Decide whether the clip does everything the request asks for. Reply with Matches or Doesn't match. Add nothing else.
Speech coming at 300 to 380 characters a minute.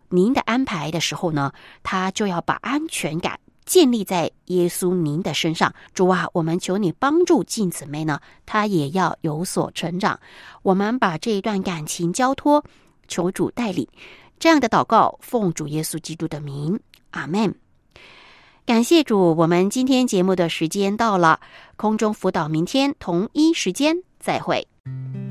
Doesn't match